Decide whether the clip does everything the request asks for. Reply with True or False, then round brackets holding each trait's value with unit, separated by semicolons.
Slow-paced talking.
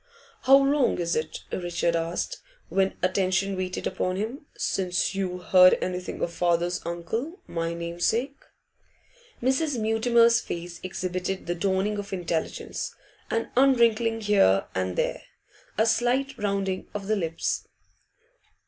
True (125 wpm)